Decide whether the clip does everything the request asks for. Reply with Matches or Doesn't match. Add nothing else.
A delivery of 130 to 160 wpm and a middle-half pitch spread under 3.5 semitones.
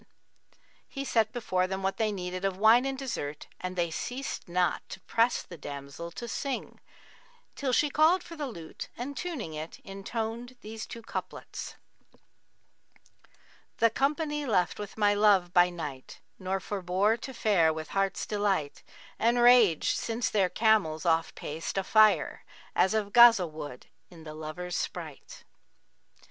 Doesn't match